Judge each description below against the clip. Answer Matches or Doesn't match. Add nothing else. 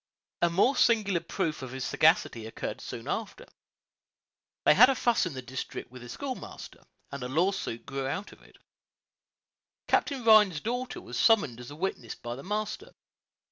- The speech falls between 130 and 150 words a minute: Doesn't match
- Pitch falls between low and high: Matches